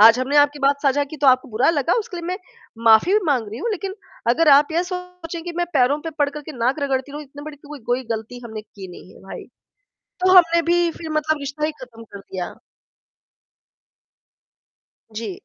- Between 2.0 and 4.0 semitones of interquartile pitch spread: No, average, 5.2 semitones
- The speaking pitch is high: Yes, very high, 290 Hz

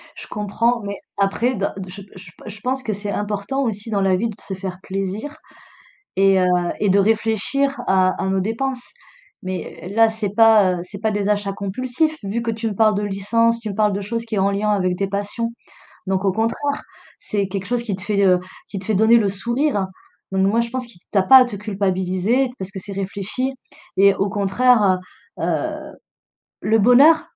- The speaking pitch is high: Yes, high, 205 Hz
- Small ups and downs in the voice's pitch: No, average, 3.0 semitones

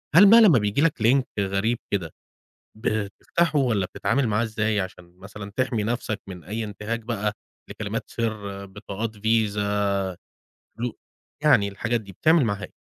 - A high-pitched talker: No, low, 110 Hz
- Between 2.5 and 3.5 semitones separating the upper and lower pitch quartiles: Yes, average, 2.9 semitones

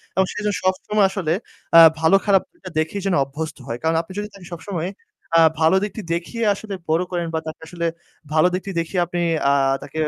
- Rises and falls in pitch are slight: No, average, 3.4 semitones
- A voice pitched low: No, medium, 180 Hz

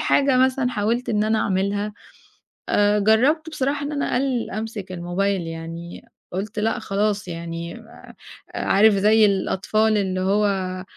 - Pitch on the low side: No, high, 210 Hz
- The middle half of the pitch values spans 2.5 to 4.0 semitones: Yes, average, 2.9 semitones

